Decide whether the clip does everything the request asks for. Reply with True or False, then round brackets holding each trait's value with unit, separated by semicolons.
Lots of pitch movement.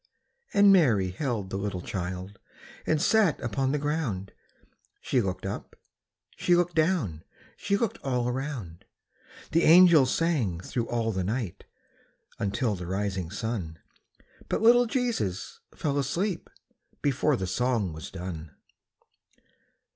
True (8.8 semitones)